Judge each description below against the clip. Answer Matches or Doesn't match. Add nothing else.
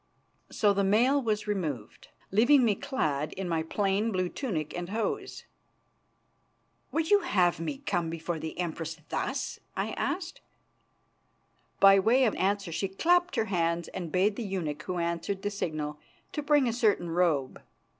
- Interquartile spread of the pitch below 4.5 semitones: Doesn't match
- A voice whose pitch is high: Matches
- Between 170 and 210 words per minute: Doesn't match